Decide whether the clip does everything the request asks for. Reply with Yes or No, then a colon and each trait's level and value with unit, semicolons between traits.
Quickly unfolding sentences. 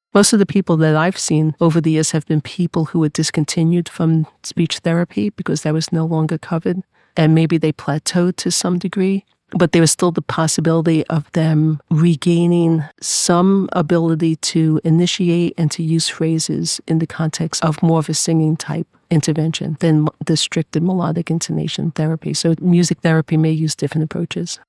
No: average, 175 wpm